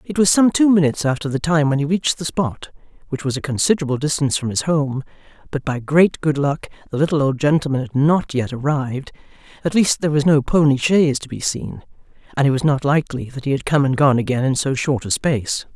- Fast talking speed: Yes, fast, 230 wpm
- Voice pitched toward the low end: No, medium, 145 Hz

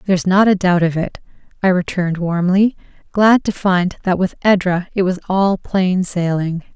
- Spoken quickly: No, average, 180 wpm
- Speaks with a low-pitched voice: No, medium, 185 Hz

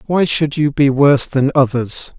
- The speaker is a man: Yes, male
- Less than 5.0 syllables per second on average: Yes, 4.6 syllables/s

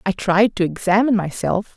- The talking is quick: No, average, 170 wpm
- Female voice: Yes, female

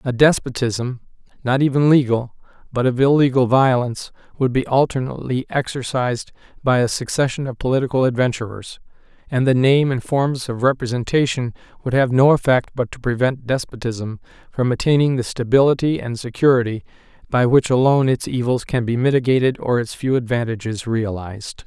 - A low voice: Yes, low, 125 Hz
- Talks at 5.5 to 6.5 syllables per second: Yes, 5.6 syllables/s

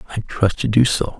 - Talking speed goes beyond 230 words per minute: No, average, 200 wpm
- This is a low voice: Yes, low, 110 Hz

